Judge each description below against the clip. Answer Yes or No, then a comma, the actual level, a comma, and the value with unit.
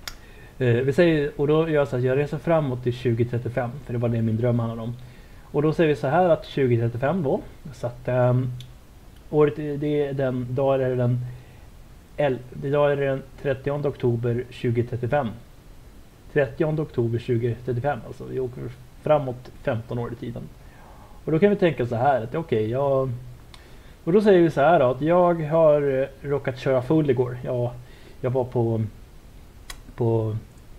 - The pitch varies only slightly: No, average, 3.2 semitones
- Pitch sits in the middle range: No, low, 130 Hz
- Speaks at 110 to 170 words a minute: No, average, 180 wpm